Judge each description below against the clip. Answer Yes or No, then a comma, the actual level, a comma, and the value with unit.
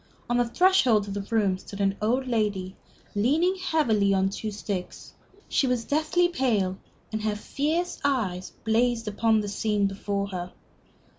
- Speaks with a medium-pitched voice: No, high, 215 Hz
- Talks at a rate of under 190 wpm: Yes, average, 155 wpm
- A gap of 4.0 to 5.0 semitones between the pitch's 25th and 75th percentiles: Yes, average, 4.4 semitones